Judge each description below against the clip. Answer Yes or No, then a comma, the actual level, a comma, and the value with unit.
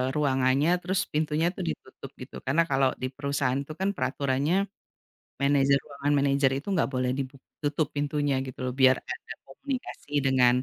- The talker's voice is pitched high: No, medium, 140 Hz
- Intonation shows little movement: Yes, narrow, 2.0 semitones